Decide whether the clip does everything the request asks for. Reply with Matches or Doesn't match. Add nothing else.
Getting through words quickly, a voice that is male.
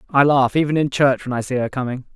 Matches